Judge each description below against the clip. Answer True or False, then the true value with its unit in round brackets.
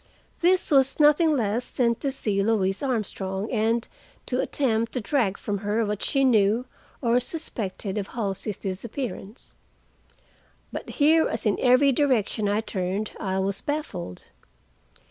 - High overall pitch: True (225 Hz)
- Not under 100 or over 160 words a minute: True (140 wpm)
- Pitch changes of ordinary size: True (4.9 semitones)